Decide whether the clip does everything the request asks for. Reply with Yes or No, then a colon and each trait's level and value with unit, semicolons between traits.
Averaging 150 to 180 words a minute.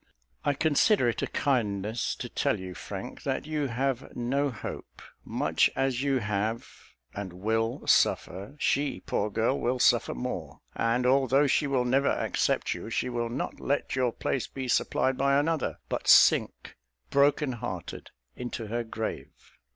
Yes: average, 155 wpm